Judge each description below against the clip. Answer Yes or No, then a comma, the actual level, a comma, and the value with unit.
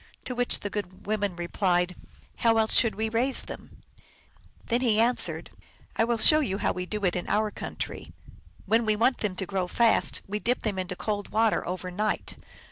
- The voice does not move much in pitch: No, average, 3.5 semitones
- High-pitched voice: Yes, high, 210 Hz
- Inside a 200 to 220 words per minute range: Yes, fast, 205 wpm